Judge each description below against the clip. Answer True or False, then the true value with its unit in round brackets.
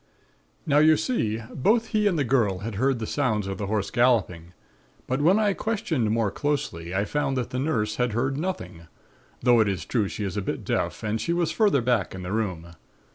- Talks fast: True (215 wpm)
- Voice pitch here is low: True (120 Hz)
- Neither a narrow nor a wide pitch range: False (6.4 semitones)